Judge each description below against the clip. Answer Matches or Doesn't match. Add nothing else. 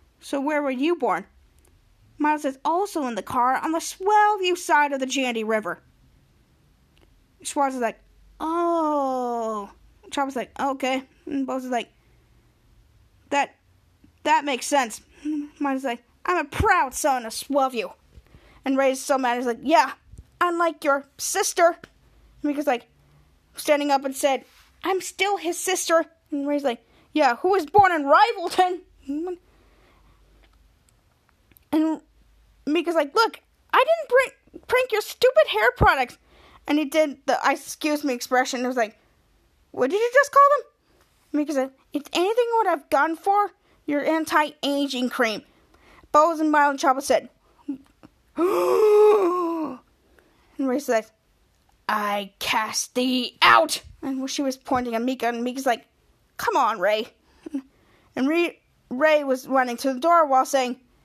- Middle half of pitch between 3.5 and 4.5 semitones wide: Matches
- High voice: Matches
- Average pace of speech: Matches